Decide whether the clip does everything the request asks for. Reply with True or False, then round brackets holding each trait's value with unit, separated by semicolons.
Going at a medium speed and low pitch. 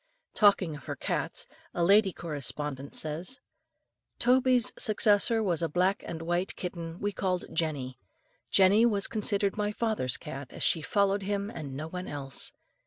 False (155 wpm; 185 Hz)